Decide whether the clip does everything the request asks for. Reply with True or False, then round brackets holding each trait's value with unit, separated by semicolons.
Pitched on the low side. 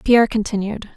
False (215 Hz)